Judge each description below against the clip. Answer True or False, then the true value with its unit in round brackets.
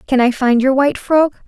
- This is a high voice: True (265 Hz)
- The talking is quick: True (245 wpm)